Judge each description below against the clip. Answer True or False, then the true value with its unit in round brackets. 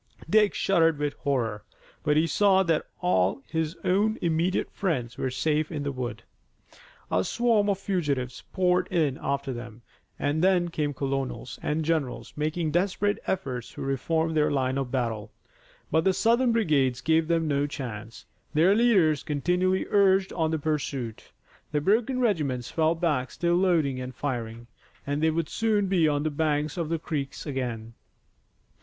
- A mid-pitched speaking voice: True (155 Hz)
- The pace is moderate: True (160 wpm)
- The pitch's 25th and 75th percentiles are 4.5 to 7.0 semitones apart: True (5.0 semitones)